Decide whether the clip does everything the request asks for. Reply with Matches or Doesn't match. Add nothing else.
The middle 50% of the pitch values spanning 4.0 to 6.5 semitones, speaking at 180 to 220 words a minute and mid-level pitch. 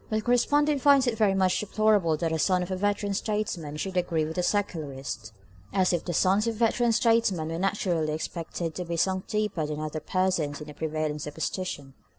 Matches